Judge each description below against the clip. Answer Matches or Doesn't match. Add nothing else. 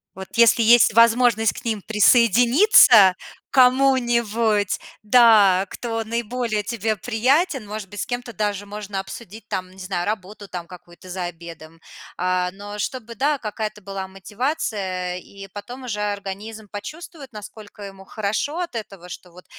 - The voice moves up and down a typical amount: Matches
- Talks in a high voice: Matches